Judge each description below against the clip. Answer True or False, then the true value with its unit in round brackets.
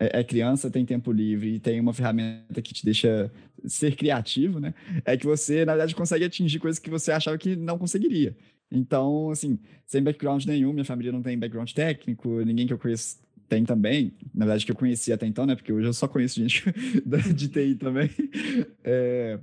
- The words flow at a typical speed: False (200 wpm)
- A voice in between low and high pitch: False (130 Hz)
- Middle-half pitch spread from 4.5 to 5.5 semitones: True (4.9 semitones)